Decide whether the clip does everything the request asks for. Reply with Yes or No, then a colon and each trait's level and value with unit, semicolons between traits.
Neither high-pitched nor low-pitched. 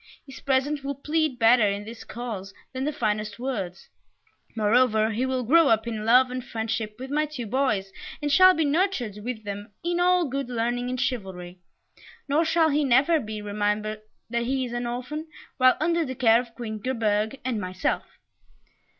No: high, 245 Hz